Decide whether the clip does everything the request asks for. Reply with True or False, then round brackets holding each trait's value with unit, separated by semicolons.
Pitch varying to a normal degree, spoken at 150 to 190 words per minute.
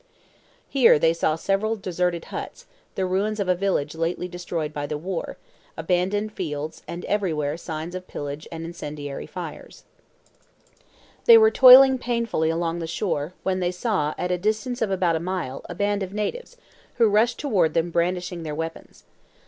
True (4.1 semitones; 165 wpm)